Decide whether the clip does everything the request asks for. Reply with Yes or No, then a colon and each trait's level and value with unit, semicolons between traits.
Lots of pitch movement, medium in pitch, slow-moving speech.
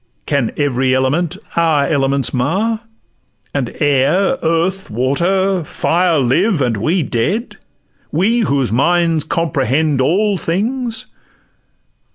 Yes: wide, 5.8 semitones; medium, 160 Hz; slow, 85 wpm